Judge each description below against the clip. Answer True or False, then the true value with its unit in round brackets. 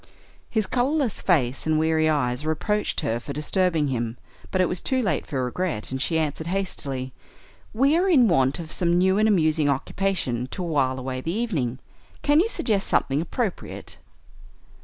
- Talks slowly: False (170 wpm)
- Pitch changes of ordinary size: False (6.6 semitones)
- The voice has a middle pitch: True (160 Hz)